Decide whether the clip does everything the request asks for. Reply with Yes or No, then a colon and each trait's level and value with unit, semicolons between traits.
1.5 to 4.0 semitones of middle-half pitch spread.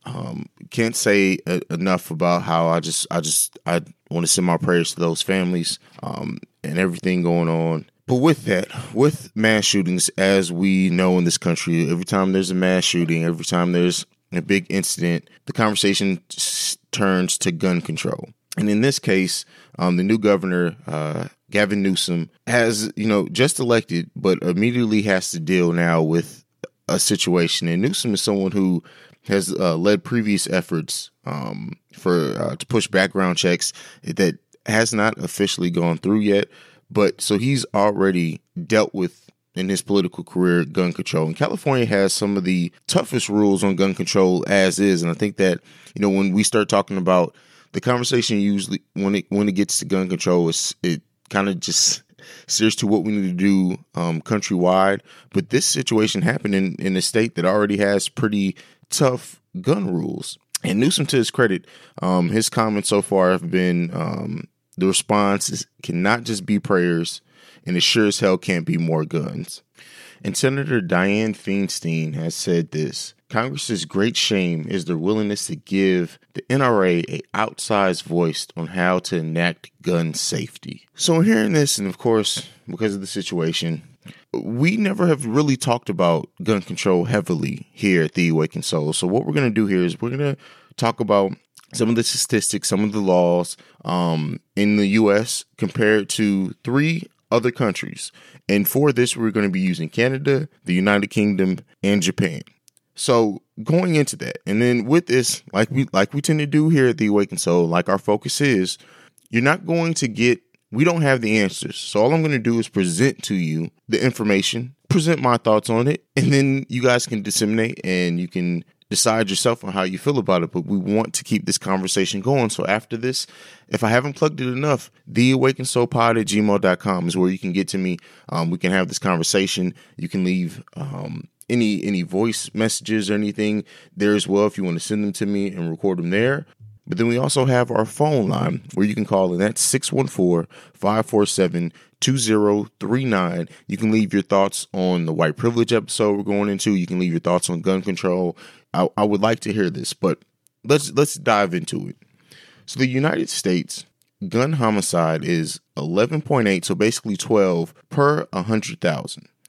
No: average, 4.5 semitones